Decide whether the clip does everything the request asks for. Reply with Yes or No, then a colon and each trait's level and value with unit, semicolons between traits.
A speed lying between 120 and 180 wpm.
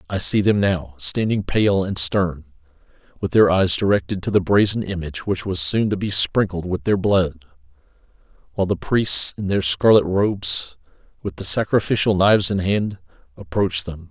Yes: average, 170 wpm